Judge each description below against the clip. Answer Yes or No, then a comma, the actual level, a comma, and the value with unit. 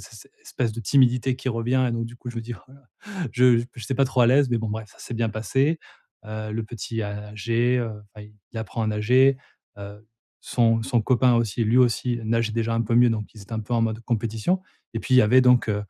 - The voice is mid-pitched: No, low, 115 Hz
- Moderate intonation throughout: No, narrow, 2.3 semitones